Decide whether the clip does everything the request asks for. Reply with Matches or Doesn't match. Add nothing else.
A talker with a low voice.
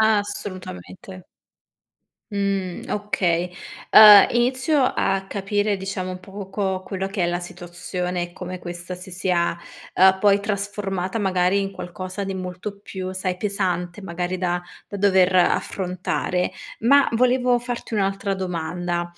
Doesn't match